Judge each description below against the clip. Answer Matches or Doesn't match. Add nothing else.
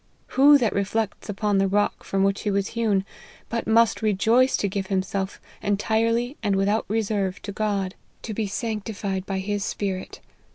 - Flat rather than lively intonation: Matches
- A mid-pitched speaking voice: Doesn't match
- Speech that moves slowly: Doesn't match